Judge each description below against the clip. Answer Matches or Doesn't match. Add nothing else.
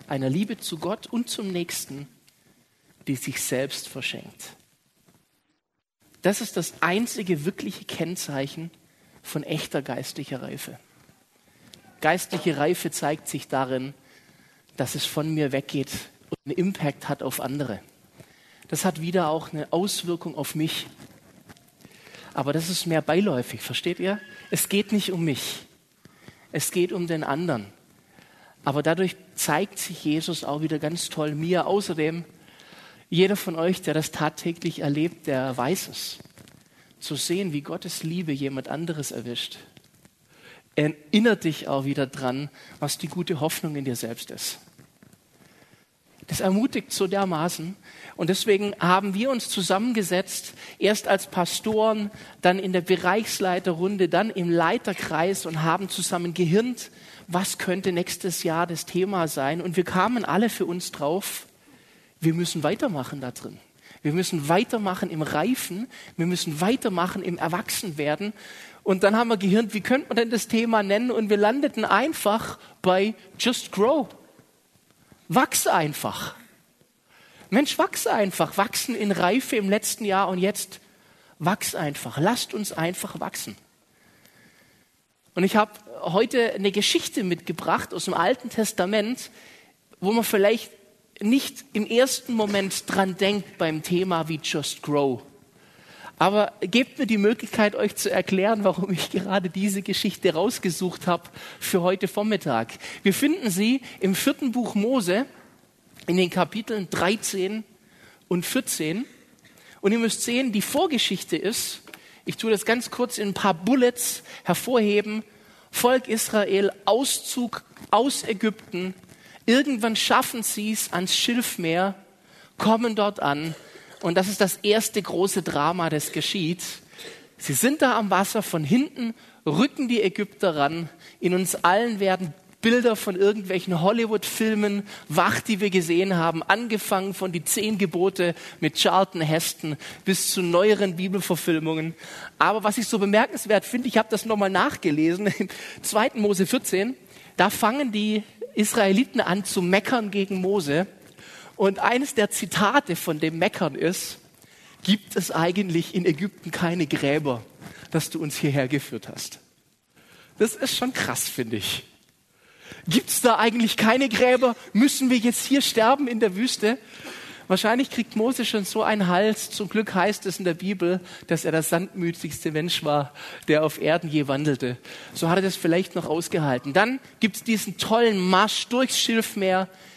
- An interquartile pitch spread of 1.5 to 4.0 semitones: Doesn't match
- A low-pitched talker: Doesn't match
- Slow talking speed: Doesn't match